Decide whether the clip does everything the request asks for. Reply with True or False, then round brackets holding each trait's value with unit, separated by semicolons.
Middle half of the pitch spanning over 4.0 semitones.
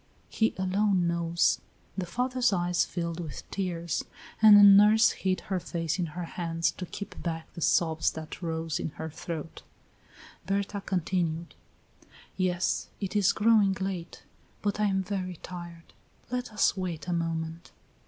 False (3.0 semitones)